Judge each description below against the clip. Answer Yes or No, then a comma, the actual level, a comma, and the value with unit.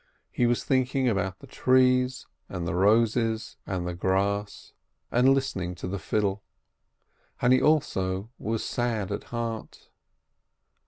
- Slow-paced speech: Yes, slow, 130 wpm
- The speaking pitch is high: No, low, 110 Hz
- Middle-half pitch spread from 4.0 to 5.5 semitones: Yes, average, 4.7 semitones